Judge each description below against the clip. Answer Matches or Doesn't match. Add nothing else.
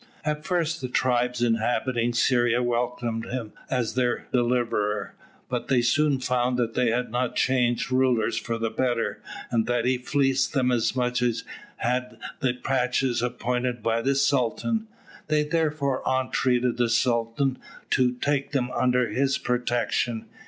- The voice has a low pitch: Matches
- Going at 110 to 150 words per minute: Matches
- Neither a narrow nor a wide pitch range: Doesn't match